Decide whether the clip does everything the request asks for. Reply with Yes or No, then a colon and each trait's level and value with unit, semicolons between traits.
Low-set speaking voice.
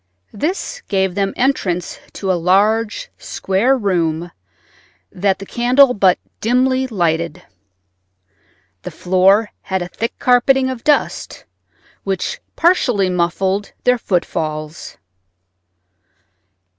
No: high, 195 Hz